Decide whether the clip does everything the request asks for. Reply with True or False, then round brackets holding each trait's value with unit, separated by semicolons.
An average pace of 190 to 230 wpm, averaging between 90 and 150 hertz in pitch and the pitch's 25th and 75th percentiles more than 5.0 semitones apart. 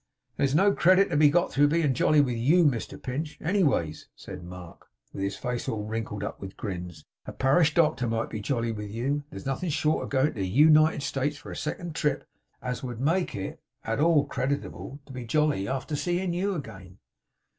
True (205 wpm; 135 Hz; 5.5 semitones)